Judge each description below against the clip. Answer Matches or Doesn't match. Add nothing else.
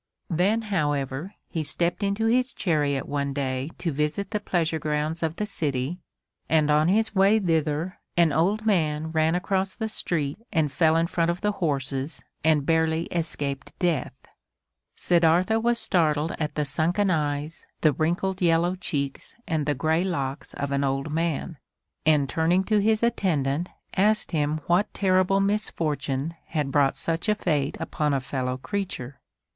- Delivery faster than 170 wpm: Doesn't match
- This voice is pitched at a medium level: Matches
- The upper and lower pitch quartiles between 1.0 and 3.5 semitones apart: Doesn't match